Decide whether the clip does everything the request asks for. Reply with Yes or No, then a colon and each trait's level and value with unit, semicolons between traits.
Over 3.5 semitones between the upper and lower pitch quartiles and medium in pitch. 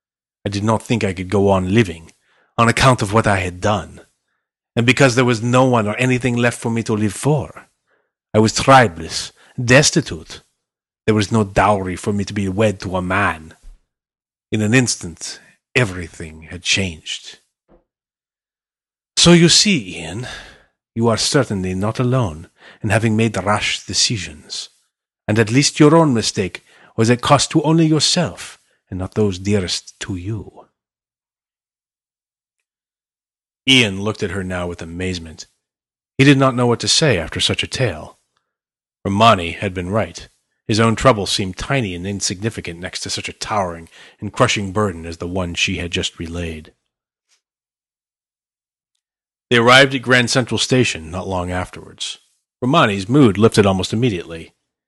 No: average, 4.9 semitones; low, 105 Hz